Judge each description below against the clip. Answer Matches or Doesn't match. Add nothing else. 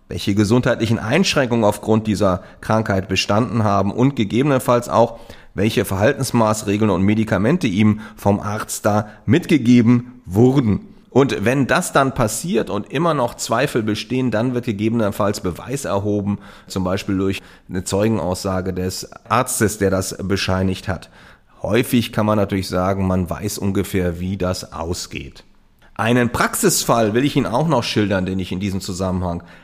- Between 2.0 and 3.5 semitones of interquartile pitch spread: Doesn't match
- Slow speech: Doesn't match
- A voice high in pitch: Doesn't match